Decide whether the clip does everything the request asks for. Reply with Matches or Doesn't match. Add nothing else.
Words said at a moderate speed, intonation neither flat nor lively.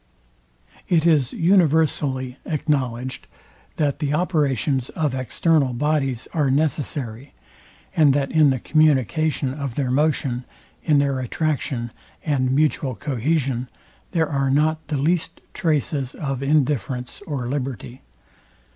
Doesn't match